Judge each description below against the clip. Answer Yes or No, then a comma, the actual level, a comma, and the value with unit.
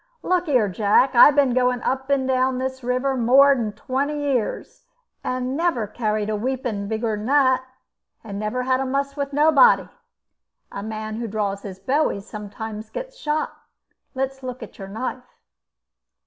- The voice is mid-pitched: No, very high, 255 Hz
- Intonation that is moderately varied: Yes, average, 4.1 semitones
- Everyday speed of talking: Yes, average, 155 wpm